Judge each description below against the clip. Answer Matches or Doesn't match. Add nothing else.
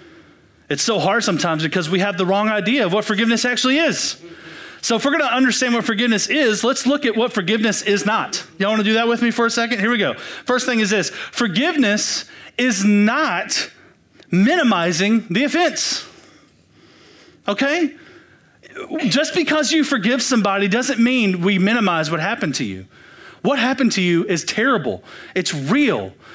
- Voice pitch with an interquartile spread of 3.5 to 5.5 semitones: Matches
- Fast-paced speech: Doesn't match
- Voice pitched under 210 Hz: Doesn't match